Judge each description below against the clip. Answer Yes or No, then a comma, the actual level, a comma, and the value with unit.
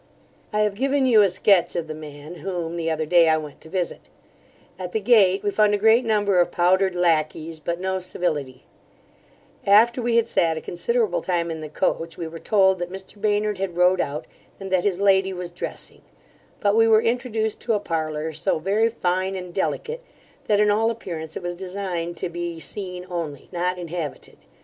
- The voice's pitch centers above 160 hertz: Yes, medium, 185 Hz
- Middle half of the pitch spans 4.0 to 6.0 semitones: No, average, 3.6 semitones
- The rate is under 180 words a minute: No, average, 195 wpm